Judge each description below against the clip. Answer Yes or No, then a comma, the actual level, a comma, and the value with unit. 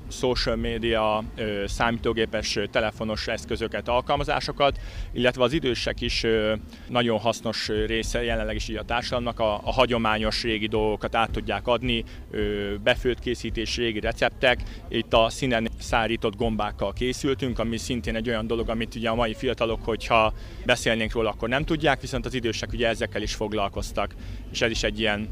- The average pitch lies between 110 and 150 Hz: Yes, low, 115 Hz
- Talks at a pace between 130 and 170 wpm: Yes, average, 150 wpm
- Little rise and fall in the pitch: Yes, narrow, 1.8 semitones